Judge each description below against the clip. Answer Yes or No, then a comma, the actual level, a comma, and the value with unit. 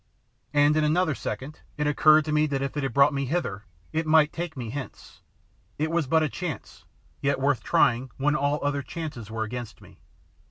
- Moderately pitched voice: Yes, medium, 145 Hz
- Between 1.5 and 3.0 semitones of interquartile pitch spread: Yes, narrow, 2.4 semitones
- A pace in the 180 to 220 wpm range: Yes, average, 200 wpm